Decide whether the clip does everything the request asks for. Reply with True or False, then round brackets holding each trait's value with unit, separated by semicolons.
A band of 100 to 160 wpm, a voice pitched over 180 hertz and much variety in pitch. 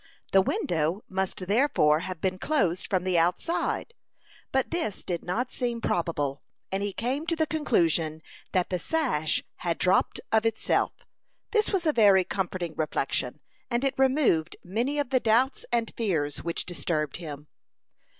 True (155 wpm; 190 Hz; 7.2 semitones)